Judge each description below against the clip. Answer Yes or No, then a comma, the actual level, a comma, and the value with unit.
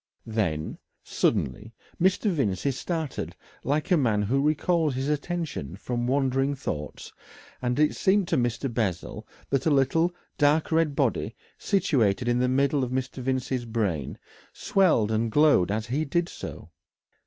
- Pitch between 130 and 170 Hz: Yes, low, 135 Hz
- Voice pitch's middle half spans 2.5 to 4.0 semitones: No, average, 4.8 semitones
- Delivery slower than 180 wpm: Yes, average, 145 wpm